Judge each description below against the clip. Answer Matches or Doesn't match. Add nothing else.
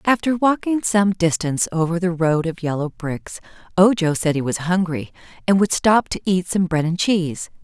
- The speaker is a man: Doesn't match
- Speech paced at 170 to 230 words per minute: Matches